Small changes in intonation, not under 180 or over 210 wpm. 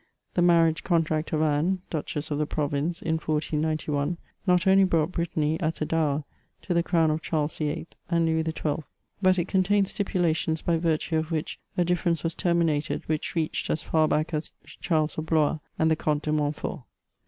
Yes: narrow, 1.7 semitones; average, 185 wpm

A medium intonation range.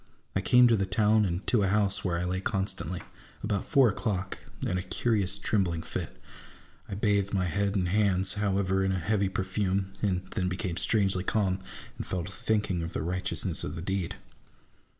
No: narrow, 2.0 semitones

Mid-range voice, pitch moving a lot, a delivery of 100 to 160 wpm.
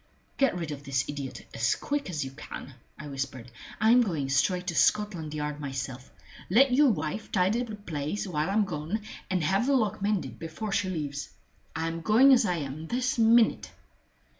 No: medium, 175 Hz; wide, 6.6 semitones; average, 180 wpm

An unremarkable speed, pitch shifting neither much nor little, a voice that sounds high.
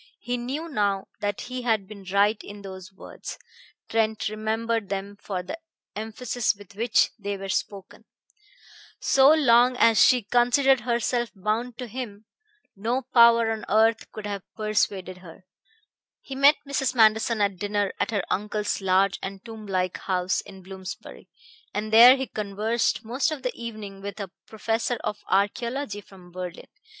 Yes: average, 155 wpm; average, 3.2 semitones; high, 215 Hz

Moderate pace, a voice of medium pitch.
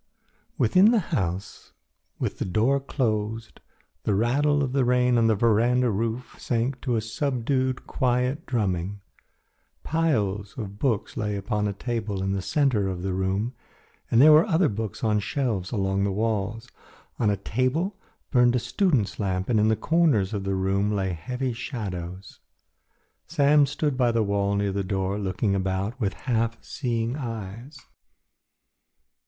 No: average, 160 wpm; low, 115 Hz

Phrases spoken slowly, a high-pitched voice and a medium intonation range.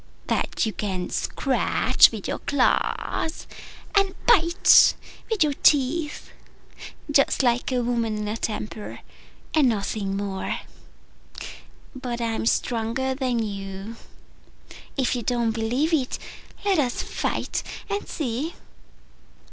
Yes: slow, 115 wpm; high, 245 Hz; average, 4.6 semitones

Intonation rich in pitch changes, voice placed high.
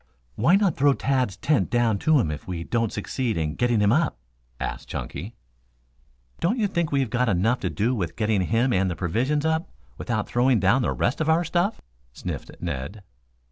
No: wide, 6.8 semitones; low, 120 Hz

